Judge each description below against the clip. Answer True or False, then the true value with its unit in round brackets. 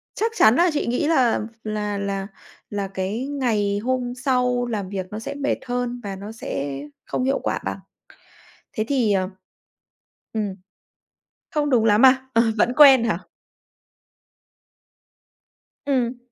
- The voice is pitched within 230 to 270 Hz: True (235 Hz)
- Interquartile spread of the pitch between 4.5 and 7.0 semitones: False (4.1 semitones)